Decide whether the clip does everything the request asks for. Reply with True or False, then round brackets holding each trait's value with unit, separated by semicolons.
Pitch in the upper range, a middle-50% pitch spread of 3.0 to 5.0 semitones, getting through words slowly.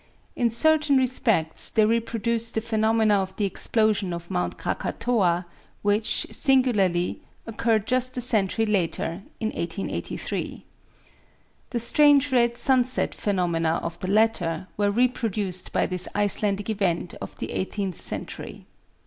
True (215 Hz; 4.2 semitones; 125 wpm)